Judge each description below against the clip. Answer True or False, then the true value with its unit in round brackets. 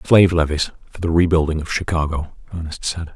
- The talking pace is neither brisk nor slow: True (170 wpm)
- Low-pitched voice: True (80 Hz)